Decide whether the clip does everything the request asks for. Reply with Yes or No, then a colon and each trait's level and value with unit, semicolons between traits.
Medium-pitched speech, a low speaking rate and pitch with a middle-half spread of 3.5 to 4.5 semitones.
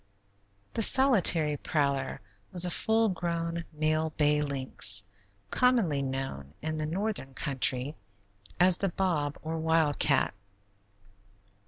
Yes: medium, 155 Hz; slow, 110 wpm; average, 4.0 semitones